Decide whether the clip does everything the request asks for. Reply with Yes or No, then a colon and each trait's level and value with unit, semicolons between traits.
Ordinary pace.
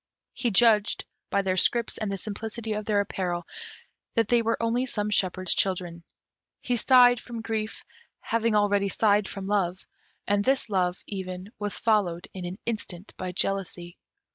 Yes: average, 160 wpm